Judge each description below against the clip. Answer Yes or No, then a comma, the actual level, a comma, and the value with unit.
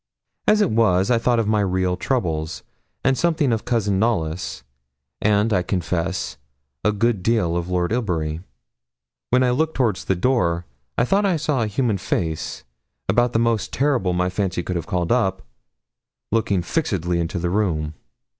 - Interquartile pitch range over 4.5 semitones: Yes, average, 5.2 semitones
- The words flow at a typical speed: Yes, average, 165 wpm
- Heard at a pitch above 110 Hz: No, low, 100 Hz